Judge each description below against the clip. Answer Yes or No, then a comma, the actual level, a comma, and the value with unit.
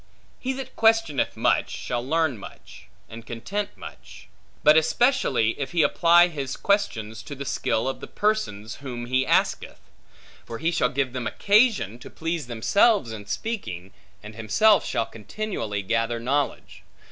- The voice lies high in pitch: No, low, 135 Hz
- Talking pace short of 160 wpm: Yes, average, 150 wpm